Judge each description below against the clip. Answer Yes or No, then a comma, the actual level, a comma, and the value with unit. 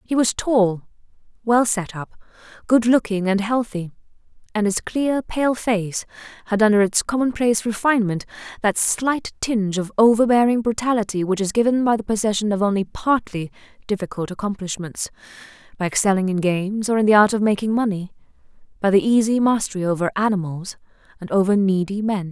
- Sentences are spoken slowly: No, average, 155 wpm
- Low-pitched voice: No, high, 210 Hz